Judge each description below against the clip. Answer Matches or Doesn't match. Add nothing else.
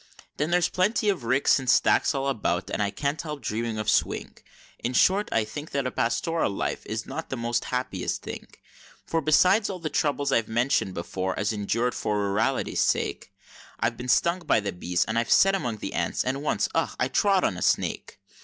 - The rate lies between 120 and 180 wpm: Doesn't match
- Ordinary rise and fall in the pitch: Doesn't match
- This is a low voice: Matches